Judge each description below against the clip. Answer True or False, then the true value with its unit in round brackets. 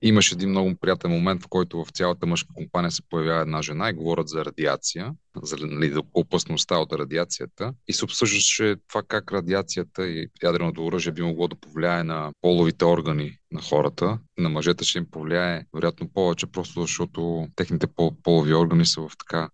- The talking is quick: True (180 wpm)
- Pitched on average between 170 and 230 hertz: False (85 Hz)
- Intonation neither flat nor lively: False (2.1 semitones)